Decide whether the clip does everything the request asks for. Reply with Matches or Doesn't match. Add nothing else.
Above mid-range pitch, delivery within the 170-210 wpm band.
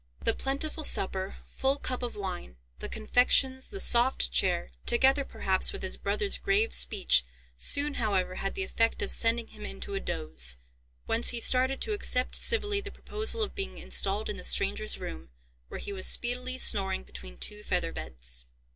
Matches